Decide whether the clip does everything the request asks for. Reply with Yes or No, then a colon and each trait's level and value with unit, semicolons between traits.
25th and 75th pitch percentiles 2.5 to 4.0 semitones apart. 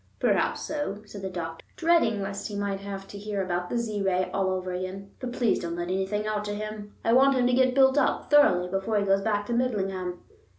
Yes: average, 3.4 semitones